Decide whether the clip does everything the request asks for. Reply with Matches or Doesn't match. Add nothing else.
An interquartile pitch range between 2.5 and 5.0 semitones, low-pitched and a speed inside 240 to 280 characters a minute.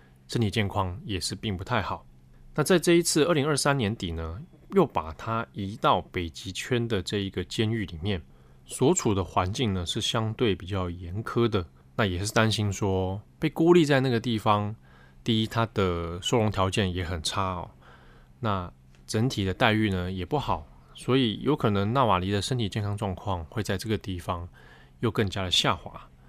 Matches